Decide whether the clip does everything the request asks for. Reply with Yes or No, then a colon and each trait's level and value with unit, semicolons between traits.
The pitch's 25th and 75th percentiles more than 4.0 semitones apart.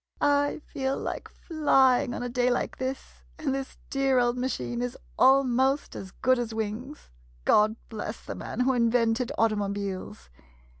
No: average, 3.6 semitones